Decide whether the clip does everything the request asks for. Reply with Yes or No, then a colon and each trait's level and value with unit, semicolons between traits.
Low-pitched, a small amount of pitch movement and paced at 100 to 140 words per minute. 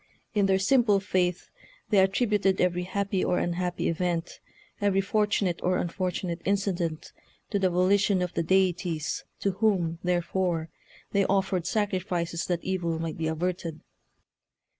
No: medium, 185 Hz; narrow, 2.3 semitones; slow, 135 wpm